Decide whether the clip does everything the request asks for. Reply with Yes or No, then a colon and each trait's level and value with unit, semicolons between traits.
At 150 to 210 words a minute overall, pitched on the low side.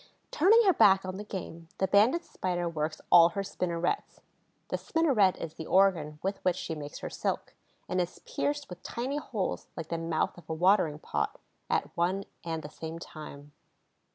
No: average, 175 wpm; medium, 180 Hz